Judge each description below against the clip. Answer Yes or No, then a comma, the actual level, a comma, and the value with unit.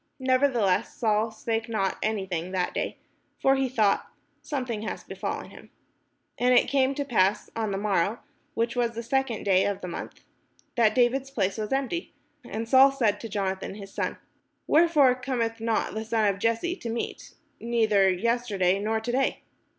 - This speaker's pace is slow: No, average, 175 wpm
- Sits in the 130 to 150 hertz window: No, high, 225 Hz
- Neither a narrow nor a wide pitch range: Yes, average, 3.9 semitones